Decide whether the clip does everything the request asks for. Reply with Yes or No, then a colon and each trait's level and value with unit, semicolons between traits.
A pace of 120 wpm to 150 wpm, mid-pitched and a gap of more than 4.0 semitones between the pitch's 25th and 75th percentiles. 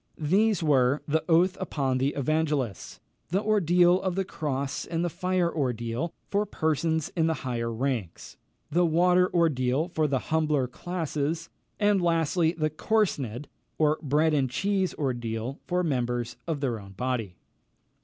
Yes: average, 145 wpm; medium, 155 Hz; average, 5.1 semitones